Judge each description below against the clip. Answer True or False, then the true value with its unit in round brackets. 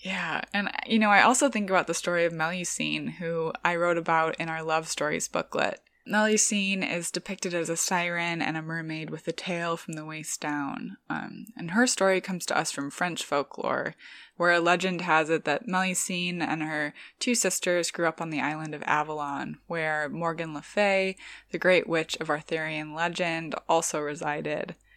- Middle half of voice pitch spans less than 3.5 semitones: True (2.7 semitones)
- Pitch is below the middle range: False (170 Hz)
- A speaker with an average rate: True (185 wpm)